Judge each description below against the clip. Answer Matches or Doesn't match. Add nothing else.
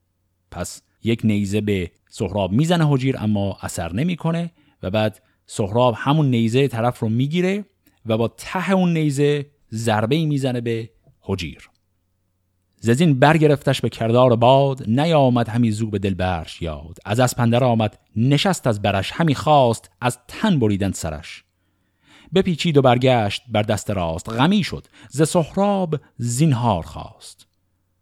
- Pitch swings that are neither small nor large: Doesn't match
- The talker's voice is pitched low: Matches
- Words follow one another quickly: Doesn't match